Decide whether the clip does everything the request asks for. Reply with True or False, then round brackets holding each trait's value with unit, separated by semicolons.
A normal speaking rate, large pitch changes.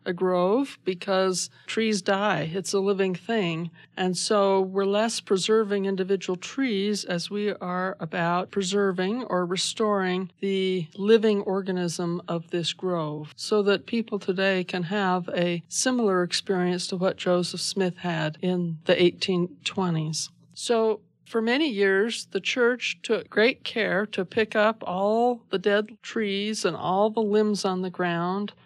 False (145 wpm; 2.6 semitones)